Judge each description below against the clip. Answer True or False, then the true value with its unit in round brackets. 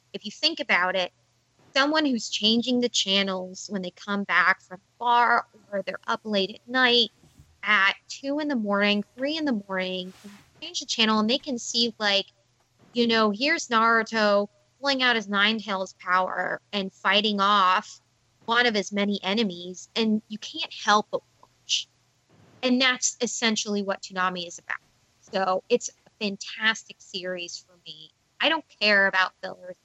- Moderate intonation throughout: True (4.1 semitones)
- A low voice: False (205 Hz)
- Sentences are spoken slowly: False (165 wpm)